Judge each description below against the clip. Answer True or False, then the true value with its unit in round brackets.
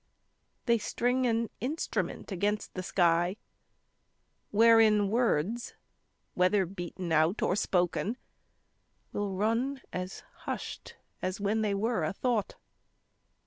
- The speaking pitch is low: False (205 Hz)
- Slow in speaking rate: True (105 wpm)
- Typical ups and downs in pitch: True (3.8 semitones)